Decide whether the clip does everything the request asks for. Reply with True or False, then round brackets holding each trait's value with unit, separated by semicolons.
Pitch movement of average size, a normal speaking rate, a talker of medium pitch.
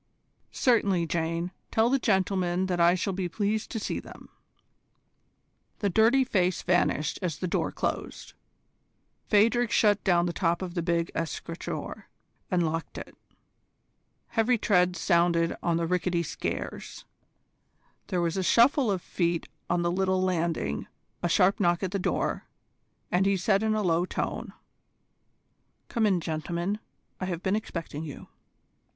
True (3.0 semitones; 145 wpm; 180 Hz)